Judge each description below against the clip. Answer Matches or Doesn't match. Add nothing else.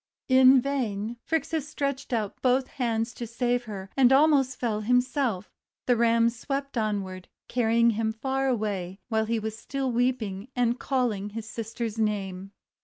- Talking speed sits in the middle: Matches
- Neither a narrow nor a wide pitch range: Matches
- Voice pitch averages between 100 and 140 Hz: Doesn't match